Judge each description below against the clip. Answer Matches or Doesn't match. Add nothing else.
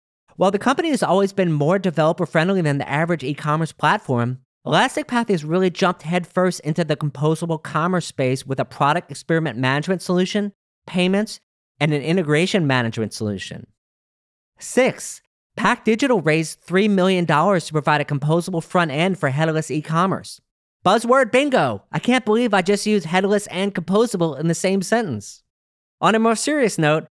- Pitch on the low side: Doesn't match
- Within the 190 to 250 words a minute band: Doesn't match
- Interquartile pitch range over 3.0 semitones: Matches